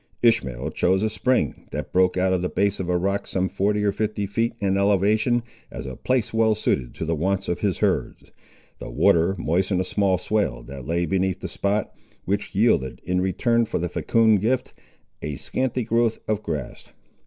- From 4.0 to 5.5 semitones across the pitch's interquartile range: No, average, 3.5 semitones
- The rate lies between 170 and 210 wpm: Yes, average, 190 wpm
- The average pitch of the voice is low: Yes, very low, 95 Hz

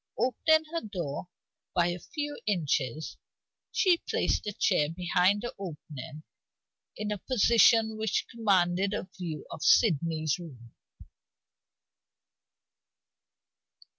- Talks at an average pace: No, slow, 105 wpm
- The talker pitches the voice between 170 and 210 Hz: Yes, medium, 185 Hz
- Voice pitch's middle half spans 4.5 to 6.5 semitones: Yes, wide, 5.6 semitones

